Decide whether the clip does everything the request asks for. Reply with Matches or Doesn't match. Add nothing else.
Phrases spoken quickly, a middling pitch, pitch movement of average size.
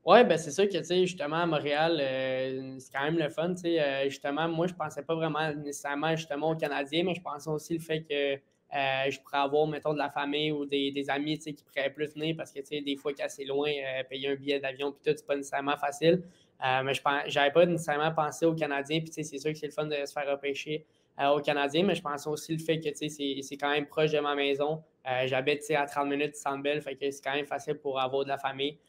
Doesn't match